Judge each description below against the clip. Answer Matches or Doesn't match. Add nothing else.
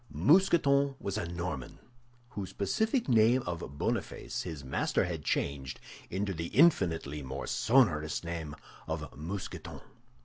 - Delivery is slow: Matches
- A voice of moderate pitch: Doesn't match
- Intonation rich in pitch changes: Matches